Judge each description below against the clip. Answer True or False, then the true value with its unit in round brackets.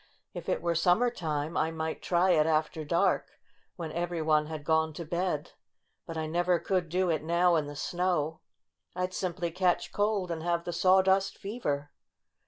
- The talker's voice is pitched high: False (170 Hz)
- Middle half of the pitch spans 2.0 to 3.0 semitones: True (2.4 semitones)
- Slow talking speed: False (180 wpm)